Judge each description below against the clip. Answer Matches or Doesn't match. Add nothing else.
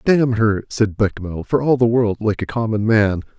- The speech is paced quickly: Matches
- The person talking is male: Matches